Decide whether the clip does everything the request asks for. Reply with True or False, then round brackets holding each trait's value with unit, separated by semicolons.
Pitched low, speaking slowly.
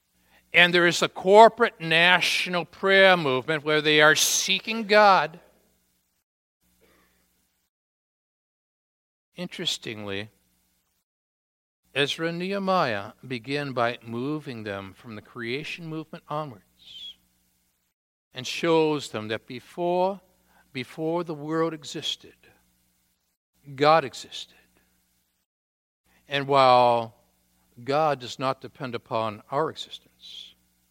True (130 Hz; 90 wpm)